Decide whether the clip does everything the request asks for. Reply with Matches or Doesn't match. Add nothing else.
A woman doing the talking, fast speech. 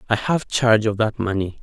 Doesn't match